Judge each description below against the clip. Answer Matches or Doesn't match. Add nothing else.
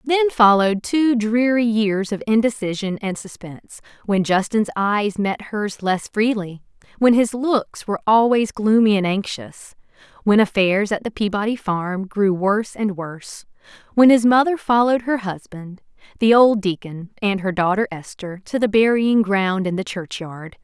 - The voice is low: Doesn't match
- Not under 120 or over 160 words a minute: Matches